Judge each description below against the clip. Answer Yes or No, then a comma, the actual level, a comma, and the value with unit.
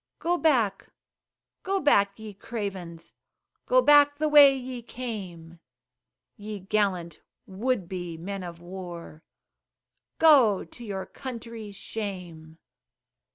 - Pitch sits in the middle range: No, high, 205 Hz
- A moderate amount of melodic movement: No, wide, 6.1 semitones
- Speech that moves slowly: Yes, slow, 110 wpm